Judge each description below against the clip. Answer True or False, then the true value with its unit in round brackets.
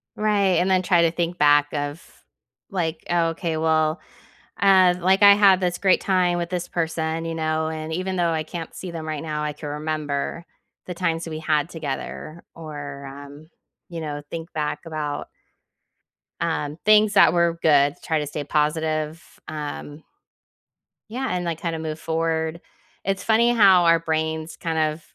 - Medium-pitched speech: True (160 Hz)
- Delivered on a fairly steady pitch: True (2.3 semitones)